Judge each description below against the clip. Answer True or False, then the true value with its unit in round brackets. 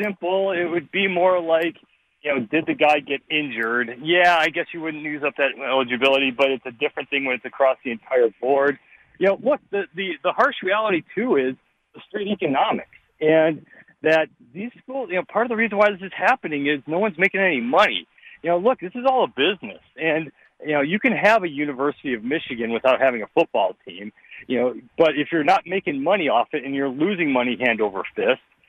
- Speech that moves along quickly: True (220 wpm)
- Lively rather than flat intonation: True (5.7 semitones)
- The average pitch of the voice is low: False (160 Hz)